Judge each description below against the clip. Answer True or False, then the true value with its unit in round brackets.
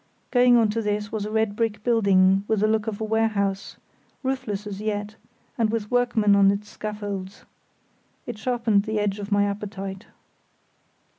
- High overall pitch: True (210 Hz)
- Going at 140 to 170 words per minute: True (165 wpm)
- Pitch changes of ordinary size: False (1.7 semitones)